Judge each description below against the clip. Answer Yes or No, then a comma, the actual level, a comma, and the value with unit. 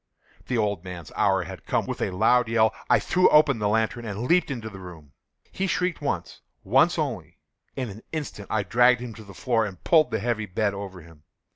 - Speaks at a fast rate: Yes, fast, 210 wpm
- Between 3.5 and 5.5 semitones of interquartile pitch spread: Yes, average, 4.1 semitones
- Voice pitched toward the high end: No, low, 110 Hz